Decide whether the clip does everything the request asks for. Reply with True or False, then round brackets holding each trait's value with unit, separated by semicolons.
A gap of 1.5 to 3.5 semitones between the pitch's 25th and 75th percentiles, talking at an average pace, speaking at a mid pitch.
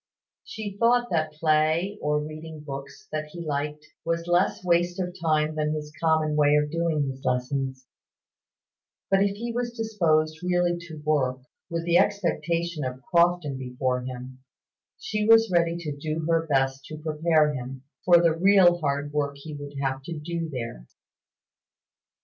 True (3.2 semitones; 160 wpm; 155 Hz)